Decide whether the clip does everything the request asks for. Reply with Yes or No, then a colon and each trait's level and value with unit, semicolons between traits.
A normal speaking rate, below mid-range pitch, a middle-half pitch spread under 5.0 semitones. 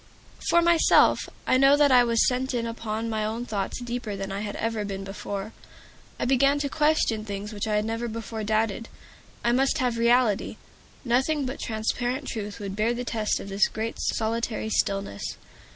No: average, 185 wpm; high, 230 Hz; average, 2.8 semitones